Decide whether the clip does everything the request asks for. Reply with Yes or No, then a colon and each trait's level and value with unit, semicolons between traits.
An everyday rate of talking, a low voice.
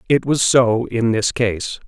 Yes: average, 190 wpm; low, 115 Hz